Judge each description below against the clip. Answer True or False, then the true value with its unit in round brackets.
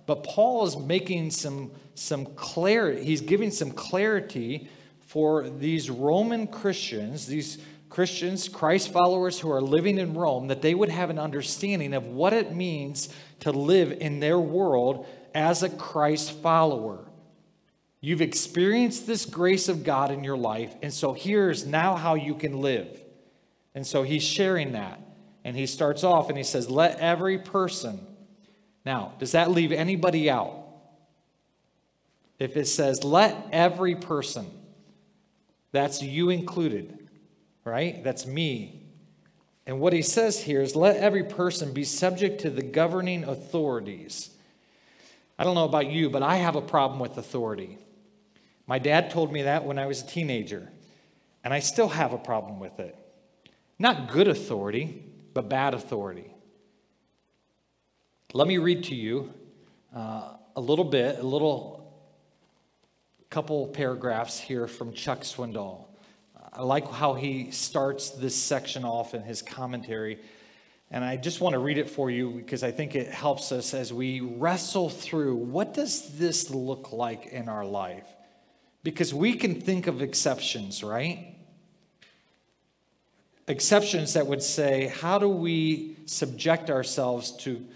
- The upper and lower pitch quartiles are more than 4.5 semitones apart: True (5.1 semitones)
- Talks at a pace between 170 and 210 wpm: False (150 wpm)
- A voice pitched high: False (155 Hz)